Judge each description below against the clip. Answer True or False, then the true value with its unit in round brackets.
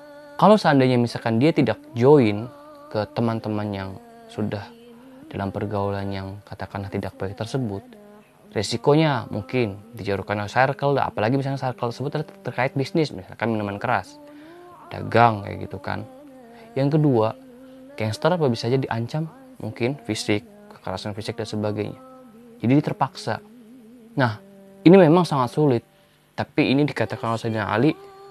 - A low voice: True (125 Hz)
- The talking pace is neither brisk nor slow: True (130 wpm)